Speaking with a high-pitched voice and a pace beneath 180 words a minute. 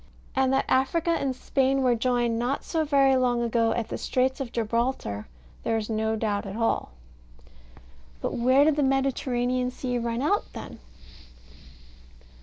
Yes: very high, 250 Hz; average, 155 wpm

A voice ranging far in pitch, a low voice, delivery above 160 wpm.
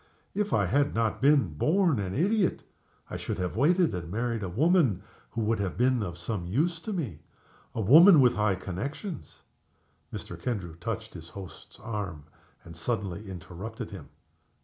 Yes: wide, 7.6 semitones; low, 110 Hz; average, 170 wpm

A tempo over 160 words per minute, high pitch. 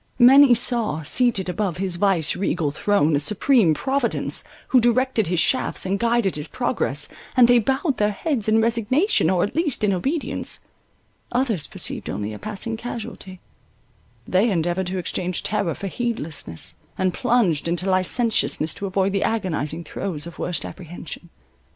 No: average, 155 wpm; high, 200 Hz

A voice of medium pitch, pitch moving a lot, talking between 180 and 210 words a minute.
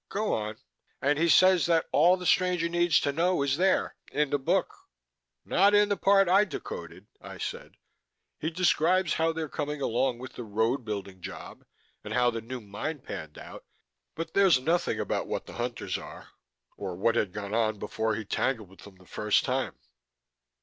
Yes: medium, 145 Hz; wide, 7.8 semitones; average, 190 wpm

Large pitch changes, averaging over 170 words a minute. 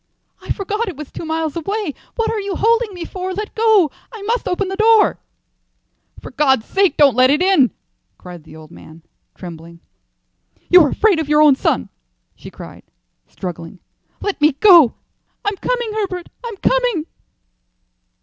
No: wide, 7.1 semitones; average, 160 wpm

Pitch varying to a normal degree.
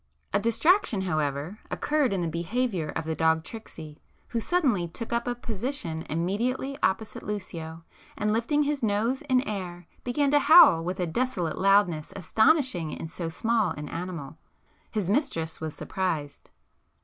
No: wide, 6.9 semitones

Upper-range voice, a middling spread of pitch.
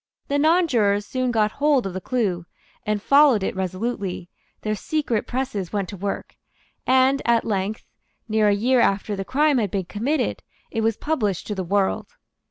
Yes: high, 215 Hz; average, 4.6 semitones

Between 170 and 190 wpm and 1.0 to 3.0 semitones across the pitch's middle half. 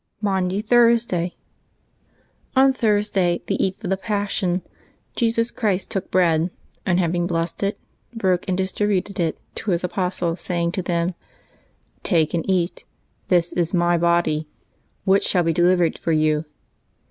No: average, 145 wpm; average, 2.7 semitones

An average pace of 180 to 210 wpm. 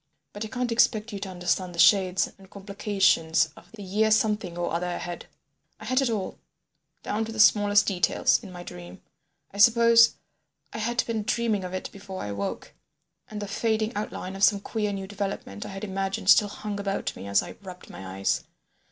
Yes: average, 195 wpm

